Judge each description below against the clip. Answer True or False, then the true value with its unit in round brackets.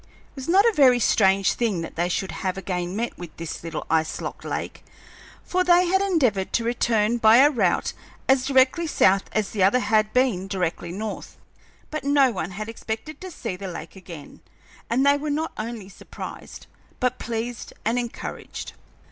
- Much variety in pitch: True (5.8 semitones)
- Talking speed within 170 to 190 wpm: True (180 wpm)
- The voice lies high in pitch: True (225 Hz)